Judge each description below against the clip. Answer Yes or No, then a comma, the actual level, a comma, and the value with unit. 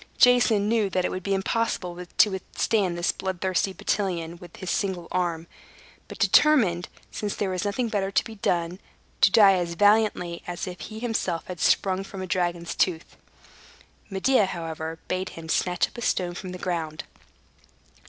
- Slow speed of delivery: No, average, 175 wpm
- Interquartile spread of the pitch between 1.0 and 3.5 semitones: Yes, average, 2.8 semitones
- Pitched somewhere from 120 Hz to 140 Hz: No, medium, 185 Hz